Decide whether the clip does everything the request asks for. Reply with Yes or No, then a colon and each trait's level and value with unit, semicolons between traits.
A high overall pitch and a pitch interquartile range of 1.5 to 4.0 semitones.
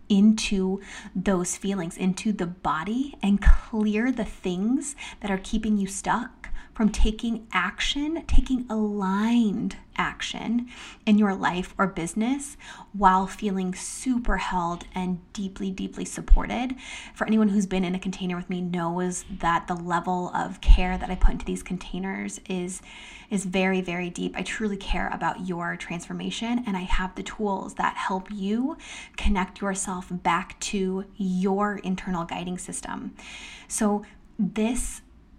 Yes: high, 195 Hz; average, 3.1 semitones